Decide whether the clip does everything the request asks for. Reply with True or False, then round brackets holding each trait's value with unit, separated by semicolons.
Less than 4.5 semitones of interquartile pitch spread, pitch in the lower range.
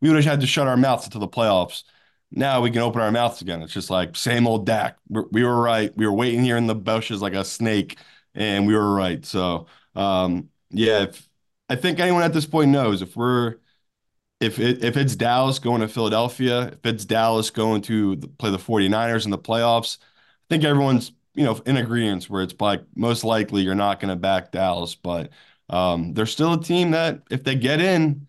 True (4.1 semitones; 115 Hz)